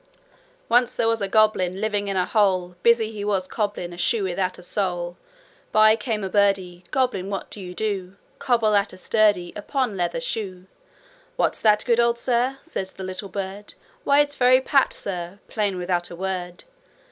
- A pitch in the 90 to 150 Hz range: No, high, 200 Hz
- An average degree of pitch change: Yes, average, 3.5 semitones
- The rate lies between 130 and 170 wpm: No, average, 185 wpm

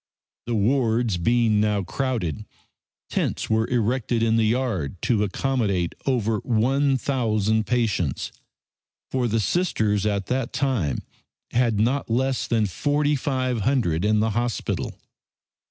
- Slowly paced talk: Yes, slow, 125 wpm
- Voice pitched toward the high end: No, low, 115 Hz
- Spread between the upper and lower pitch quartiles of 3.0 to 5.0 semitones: Yes, average, 3.5 semitones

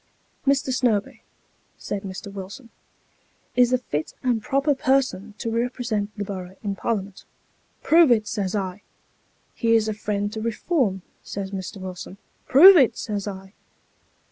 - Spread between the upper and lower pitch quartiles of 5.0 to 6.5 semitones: No, average, 4.1 semitones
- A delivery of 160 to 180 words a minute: Yes, average, 165 wpm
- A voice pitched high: Yes, high, 215 Hz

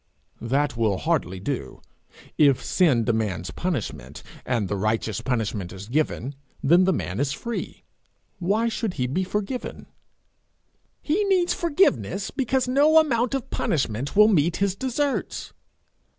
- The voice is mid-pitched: Yes, medium, 155 Hz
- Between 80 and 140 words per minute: Yes, slow, 135 wpm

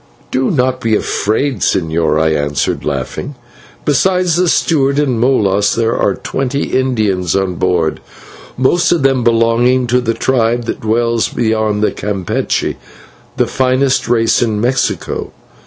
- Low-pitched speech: Yes, low, 120 Hz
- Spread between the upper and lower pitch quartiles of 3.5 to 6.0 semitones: Yes, average, 3.9 semitones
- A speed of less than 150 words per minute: Yes, slow, 135 wpm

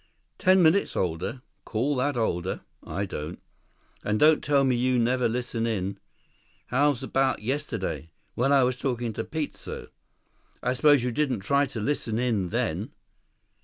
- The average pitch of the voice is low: Yes, low, 125 Hz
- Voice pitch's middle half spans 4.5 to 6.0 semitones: No, average, 3.9 semitones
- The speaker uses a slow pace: No, average, 150 wpm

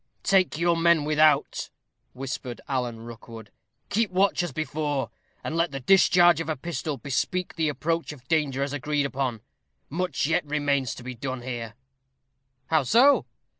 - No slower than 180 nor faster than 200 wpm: No, average, 155 wpm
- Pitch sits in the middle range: Yes, medium, 150 Hz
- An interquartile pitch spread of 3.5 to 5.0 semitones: Yes, average, 4.4 semitones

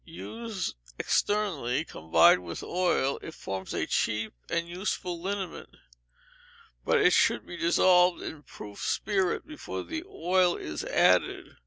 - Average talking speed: No, slow, 130 wpm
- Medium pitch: Yes, medium, 175 Hz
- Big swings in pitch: Yes, wide, 6.6 semitones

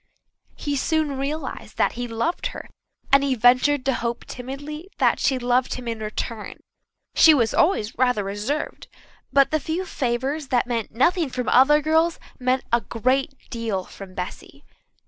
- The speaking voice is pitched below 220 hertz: No, very high, 260 Hz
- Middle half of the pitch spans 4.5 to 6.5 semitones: No, average, 3.8 semitones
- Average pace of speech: Yes, average, 160 wpm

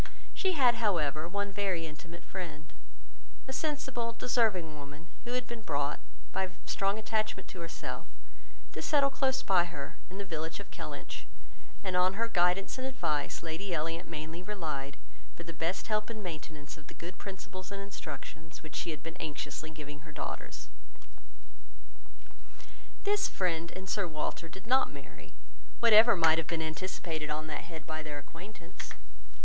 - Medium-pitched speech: Yes, medium, 175 Hz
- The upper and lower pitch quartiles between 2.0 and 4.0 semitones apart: No, average, 4.5 semitones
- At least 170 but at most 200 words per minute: No, average, 160 wpm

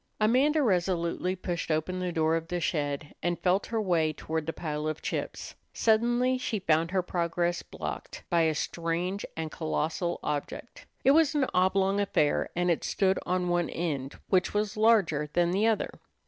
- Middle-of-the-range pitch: Yes, medium, 175 Hz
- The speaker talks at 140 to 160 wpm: No, average, 175 wpm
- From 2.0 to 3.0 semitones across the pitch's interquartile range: No, average, 3.6 semitones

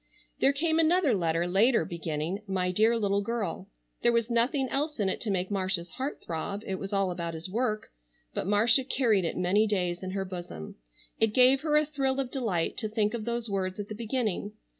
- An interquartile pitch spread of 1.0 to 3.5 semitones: No, average, 4.7 semitones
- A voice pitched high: Yes, high, 210 Hz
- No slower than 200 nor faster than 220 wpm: Yes, fast, 205 wpm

